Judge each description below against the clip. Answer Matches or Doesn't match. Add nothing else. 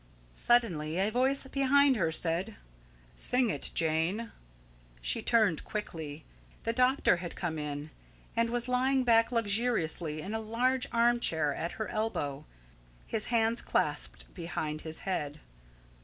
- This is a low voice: Doesn't match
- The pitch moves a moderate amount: Doesn't match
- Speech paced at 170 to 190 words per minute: Doesn't match